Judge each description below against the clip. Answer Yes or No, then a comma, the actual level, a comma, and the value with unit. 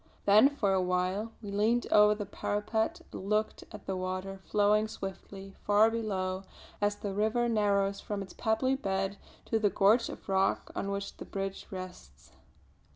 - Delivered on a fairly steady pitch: Yes, narrow, 1.9 semitones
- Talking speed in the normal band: Yes, average, 165 wpm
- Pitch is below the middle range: No, high, 205 Hz